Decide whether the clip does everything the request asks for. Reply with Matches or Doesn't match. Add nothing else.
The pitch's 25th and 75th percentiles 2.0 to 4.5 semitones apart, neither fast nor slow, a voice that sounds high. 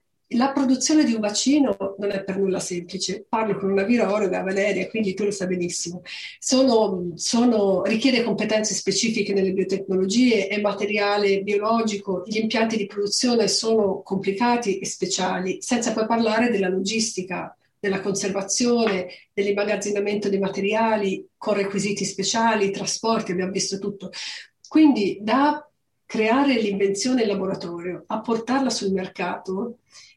Matches